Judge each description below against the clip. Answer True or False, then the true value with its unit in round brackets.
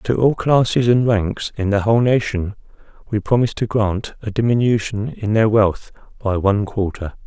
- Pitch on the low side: True (110 Hz)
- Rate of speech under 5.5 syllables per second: True (5.0 syllables/s)